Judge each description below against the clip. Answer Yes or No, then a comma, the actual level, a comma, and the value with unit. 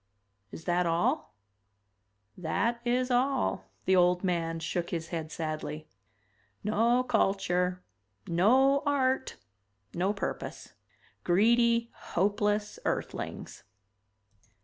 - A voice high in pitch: Yes, high, 195 Hz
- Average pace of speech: No, slow, 90 wpm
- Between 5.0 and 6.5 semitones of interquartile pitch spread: Yes, wide, 5.6 semitones